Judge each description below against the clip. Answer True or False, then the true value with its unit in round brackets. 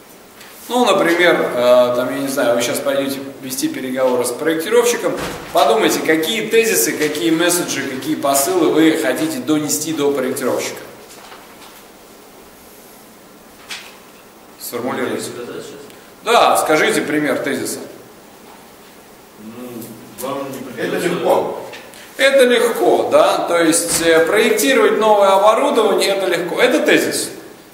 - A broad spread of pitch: True (7.8 semitones)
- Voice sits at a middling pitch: True (160 Hz)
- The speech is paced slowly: True (95 wpm)